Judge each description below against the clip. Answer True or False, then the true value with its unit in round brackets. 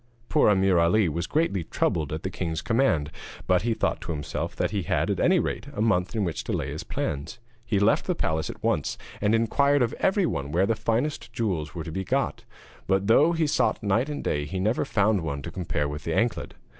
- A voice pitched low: True (95 Hz)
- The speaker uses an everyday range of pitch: False (5.8 semitones)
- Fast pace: True (225 wpm)